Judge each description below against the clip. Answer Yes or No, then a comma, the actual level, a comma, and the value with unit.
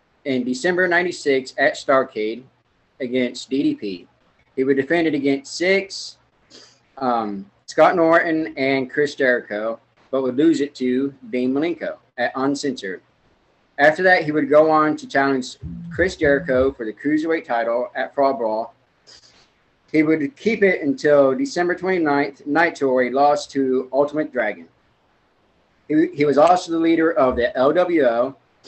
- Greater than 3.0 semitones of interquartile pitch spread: Yes, average, 4.0 semitones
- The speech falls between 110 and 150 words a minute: Yes, average, 140 wpm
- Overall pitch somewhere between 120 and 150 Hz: Yes, medium, 140 Hz